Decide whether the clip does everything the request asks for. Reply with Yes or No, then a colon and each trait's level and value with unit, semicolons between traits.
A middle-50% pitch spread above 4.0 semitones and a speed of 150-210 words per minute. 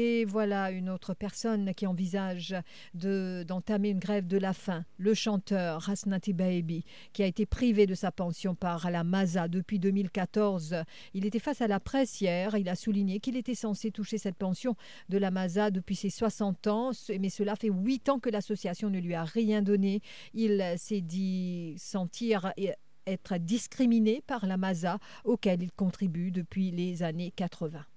No: narrow, 2.4 semitones; average, 175 wpm